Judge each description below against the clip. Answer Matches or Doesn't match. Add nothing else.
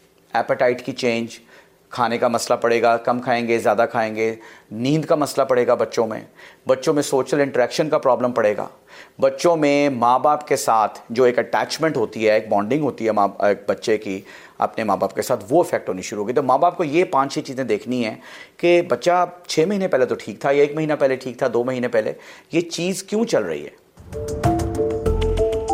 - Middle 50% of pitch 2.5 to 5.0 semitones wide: Doesn't match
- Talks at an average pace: Doesn't match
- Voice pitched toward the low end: Matches